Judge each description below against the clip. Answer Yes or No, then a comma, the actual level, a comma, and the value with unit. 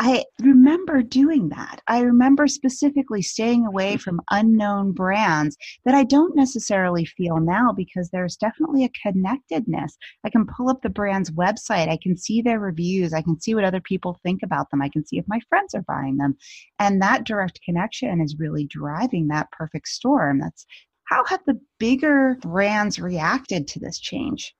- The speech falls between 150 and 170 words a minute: No, average, 180 wpm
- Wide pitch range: Yes, wide, 6.2 semitones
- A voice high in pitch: Yes, high, 205 Hz